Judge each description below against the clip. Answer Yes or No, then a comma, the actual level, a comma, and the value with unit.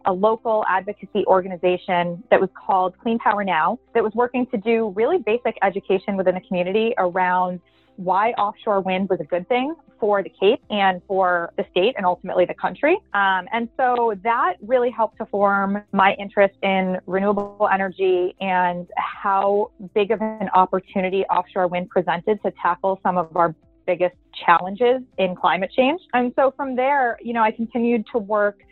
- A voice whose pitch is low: No, high, 195 Hz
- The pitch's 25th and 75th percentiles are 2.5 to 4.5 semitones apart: Yes, average, 3.5 semitones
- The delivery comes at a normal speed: Yes, average, 170 wpm